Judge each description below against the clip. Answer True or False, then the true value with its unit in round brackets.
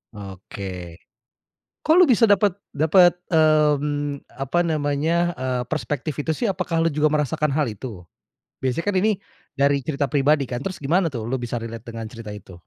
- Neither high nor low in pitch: True (145 Hz)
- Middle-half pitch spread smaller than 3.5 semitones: False (4.2 semitones)